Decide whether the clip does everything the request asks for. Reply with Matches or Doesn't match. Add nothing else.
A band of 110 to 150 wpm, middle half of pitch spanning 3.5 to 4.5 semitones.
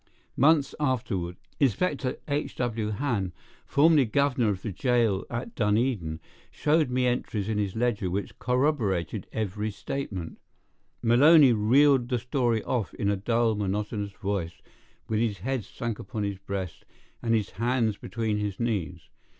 Matches